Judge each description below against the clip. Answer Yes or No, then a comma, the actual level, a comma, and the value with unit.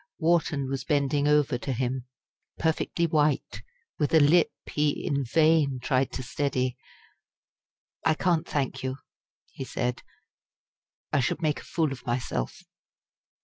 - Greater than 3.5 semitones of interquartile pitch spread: No, average, 3.1 semitones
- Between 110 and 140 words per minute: Yes, slow, 135 wpm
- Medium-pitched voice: Yes, medium, 145 Hz